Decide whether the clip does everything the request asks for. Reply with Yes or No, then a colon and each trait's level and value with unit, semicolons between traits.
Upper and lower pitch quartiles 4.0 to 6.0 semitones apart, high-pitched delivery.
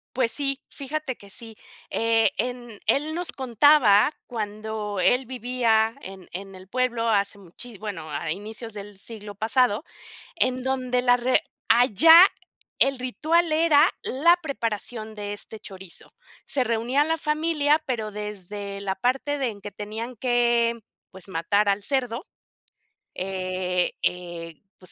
Yes: average, 4.3 semitones; high, 230 Hz